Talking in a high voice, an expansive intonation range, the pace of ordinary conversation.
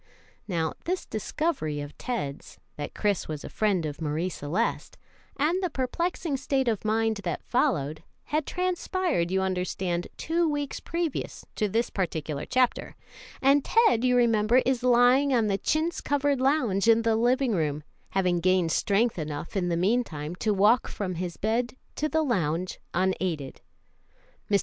Yes: high, 220 Hz; wide, 7.1 semitones; average, 160 wpm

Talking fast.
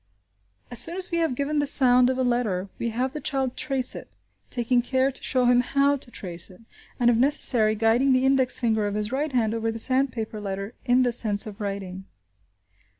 Yes: fast, 210 wpm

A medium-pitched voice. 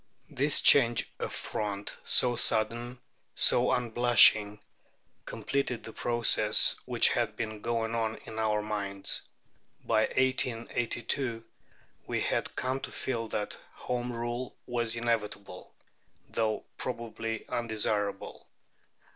No: low, 115 Hz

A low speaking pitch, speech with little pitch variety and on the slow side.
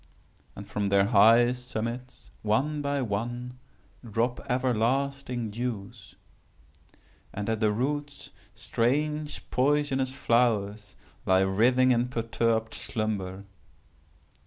No: low, 120 Hz; average, 3.3 semitones; slow, 95 wpm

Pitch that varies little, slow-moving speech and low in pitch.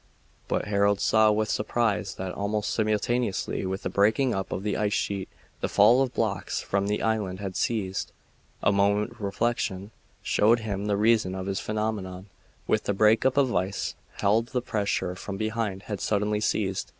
No: narrow, 1.9 semitones; average, 175 wpm; low, 105 Hz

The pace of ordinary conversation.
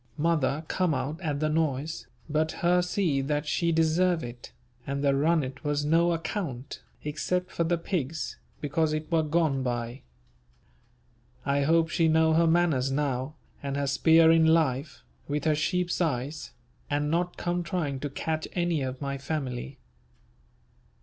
Yes: average, 155 wpm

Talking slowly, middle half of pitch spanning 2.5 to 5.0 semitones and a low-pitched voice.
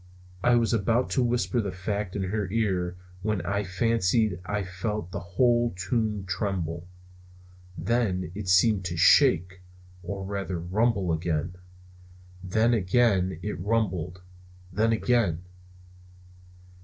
Yes: slow, 120 wpm; average, 3.7 semitones; low, 100 Hz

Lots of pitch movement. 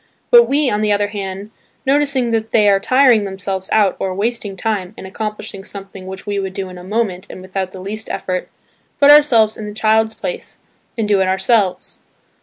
No: average, 2.7 semitones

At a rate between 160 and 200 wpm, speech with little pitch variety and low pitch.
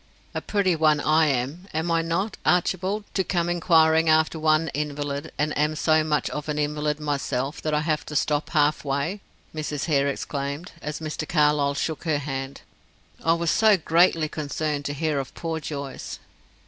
No: average, 175 wpm; narrow, 2.0 semitones; medium, 155 Hz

